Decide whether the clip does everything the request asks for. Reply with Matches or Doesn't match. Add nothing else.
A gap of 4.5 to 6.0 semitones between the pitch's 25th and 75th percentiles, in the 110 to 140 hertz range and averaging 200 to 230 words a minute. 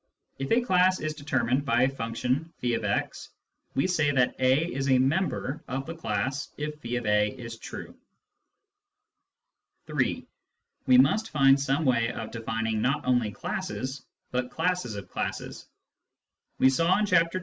Doesn't match